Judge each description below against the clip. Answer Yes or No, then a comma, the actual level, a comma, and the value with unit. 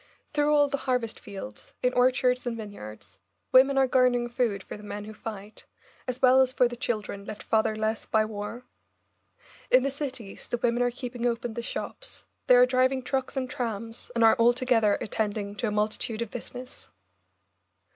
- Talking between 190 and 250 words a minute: No, average, 175 wpm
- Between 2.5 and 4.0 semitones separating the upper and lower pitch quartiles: Yes, average, 2.9 semitones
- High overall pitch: Yes, high, 240 Hz